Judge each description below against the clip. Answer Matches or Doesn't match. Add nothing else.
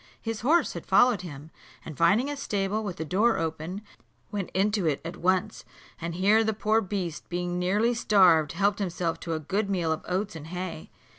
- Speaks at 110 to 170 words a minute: Doesn't match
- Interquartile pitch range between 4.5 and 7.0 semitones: Doesn't match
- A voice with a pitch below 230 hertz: Matches